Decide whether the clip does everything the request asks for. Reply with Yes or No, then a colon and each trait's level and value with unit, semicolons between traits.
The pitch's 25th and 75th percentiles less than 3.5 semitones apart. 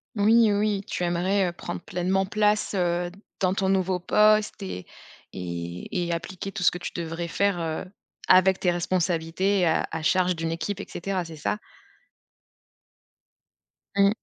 Yes: narrow, 2.5 semitones